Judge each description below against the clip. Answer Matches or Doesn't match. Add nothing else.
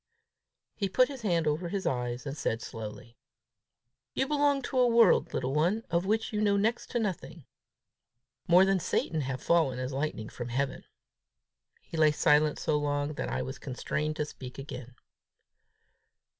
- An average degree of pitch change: Doesn't match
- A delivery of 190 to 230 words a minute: Doesn't match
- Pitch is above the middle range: Doesn't match